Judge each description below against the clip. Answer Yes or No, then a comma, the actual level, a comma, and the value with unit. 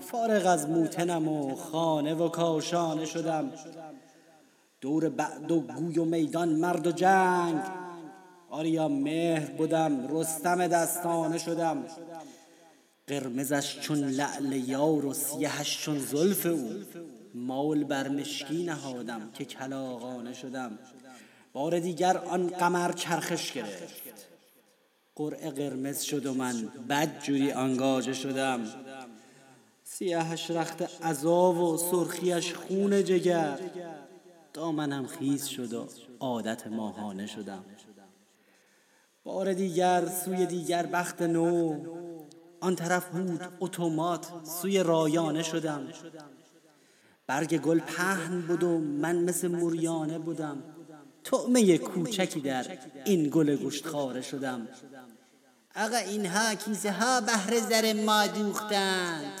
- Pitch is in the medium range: Yes, medium, 165 Hz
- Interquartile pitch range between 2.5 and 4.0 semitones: Yes, average, 3.4 semitones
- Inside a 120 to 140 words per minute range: No, average, 110 wpm